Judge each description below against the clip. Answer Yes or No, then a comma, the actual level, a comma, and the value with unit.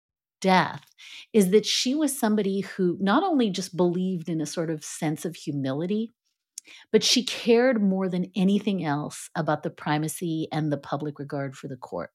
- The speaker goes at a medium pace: Yes, average, 175 wpm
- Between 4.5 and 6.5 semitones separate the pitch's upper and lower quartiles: Yes, wide, 5.6 semitones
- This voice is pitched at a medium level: Yes, medium, 180 Hz